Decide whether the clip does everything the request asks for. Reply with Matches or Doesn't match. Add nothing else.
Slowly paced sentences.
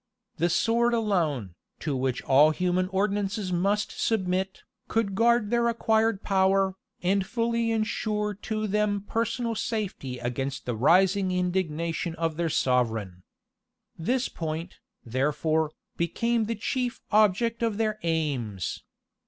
Matches